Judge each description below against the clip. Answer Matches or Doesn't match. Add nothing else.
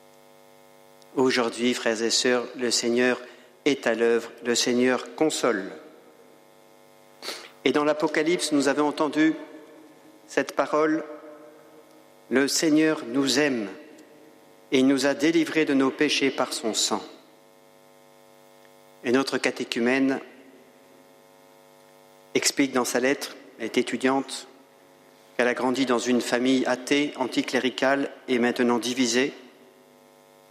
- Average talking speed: Doesn't match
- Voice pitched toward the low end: Matches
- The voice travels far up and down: Doesn't match